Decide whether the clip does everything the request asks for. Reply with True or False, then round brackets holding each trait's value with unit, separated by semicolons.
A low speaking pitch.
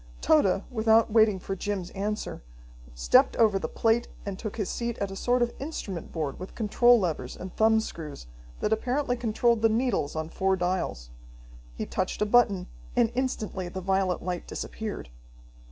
False (205 Hz)